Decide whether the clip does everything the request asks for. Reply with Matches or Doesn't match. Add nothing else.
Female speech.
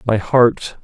Doesn't match